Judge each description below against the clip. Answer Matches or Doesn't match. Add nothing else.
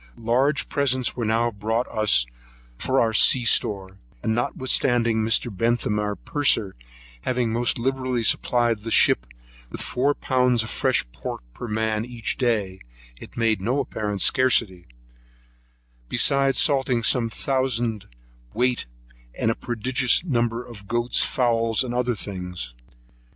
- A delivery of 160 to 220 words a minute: Doesn't match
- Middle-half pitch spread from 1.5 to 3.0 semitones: Matches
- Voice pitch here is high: Doesn't match